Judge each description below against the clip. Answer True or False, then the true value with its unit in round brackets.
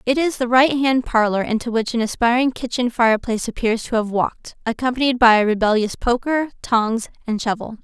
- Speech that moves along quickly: False (175 wpm)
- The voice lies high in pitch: True (235 Hz)